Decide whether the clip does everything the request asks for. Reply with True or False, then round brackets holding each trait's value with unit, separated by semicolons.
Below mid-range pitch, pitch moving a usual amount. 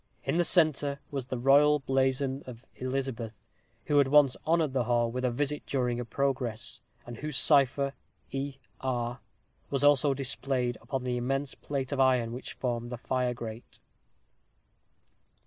False (130 Hz; 2.3 semitones)